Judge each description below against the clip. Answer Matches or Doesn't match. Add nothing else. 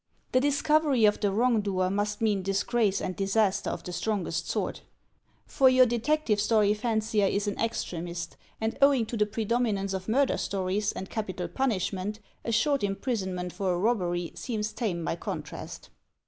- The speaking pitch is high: Matches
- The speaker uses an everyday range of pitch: Matches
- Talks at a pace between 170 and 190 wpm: Doesn't match